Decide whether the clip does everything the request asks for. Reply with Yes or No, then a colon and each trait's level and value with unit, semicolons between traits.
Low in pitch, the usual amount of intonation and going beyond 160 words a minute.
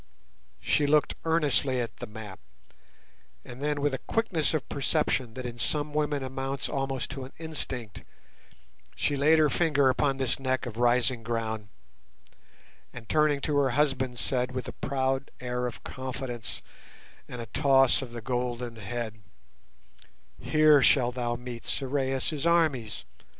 No: low, 130 Hz; average, 3.0 semitones; average, 145 wpm